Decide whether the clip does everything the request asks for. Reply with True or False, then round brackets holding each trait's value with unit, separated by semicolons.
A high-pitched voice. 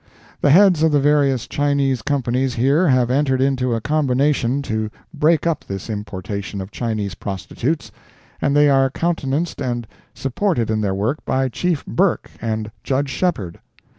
False (135 Hz)